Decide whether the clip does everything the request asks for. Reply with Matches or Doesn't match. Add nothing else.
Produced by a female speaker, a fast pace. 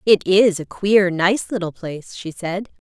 Doesn't match